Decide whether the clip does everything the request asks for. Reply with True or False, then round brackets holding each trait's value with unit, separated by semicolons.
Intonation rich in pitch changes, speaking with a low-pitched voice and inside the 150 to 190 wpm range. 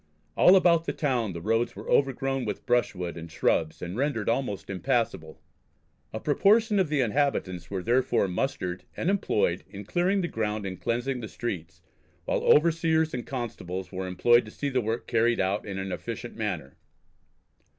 True (6.5 semitones; 115 Hz; 170 wpm)